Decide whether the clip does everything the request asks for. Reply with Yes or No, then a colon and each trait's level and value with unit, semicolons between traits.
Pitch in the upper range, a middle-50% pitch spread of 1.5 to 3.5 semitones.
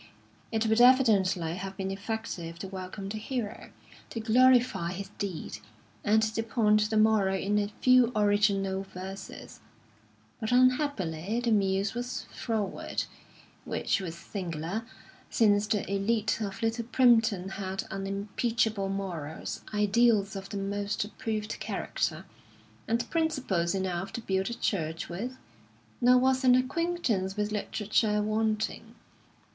Yes: high, 210 Hz; average, 2.8 semitones